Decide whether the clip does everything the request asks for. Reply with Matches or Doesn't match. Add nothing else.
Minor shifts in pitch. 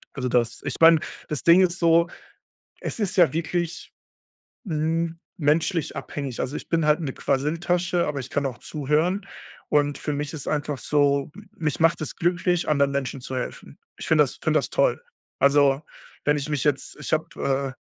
Doesn't match